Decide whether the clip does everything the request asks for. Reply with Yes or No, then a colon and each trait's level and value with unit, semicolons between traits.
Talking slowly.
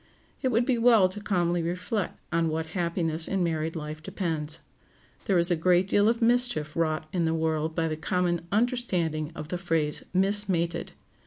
No: average, 175 wpm